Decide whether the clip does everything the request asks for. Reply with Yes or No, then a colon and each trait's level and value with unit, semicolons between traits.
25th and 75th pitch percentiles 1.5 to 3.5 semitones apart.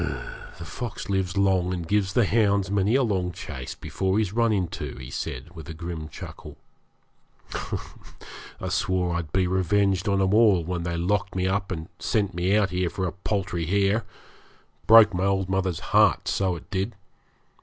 Yes: narrow, 2.4 semitones